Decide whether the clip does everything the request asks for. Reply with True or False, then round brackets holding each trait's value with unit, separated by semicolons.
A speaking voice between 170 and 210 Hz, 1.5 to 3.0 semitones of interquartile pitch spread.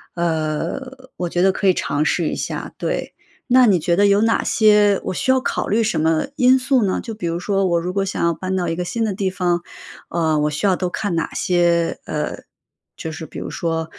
False (185 Hz; 3.8 semitones)